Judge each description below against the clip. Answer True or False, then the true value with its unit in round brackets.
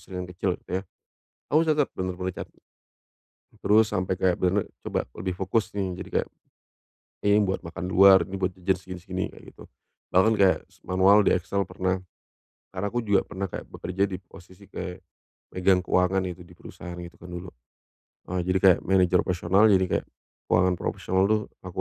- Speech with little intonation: True (1.2 semitones)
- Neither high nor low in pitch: False (95 Hz)